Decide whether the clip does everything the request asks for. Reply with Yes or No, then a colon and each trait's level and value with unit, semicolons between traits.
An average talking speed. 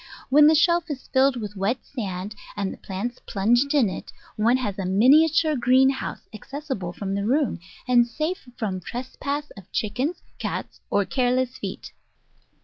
Yes: average, 160 wpm